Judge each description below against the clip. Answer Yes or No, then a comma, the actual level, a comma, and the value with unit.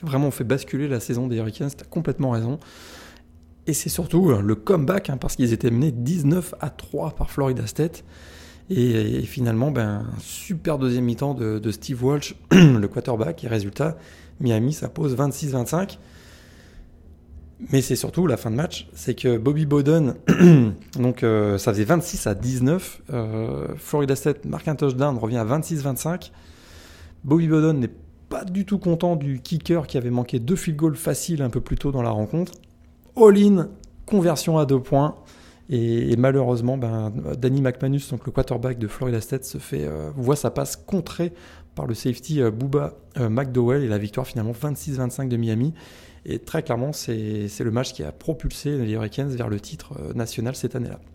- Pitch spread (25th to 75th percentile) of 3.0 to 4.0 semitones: No, average, 4.7 semitones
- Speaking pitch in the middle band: No, low, 130 Hz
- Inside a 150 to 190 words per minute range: Yes, average, 180 wpm